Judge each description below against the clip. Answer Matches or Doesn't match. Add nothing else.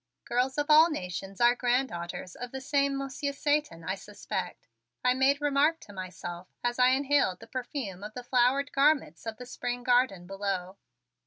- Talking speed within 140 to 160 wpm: Doesn't match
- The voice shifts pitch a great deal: Matches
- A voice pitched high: Matches